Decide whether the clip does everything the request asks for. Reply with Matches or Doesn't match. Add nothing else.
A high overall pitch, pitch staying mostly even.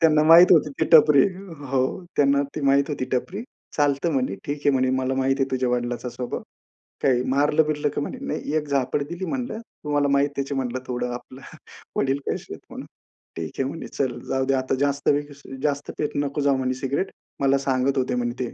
Doesn't match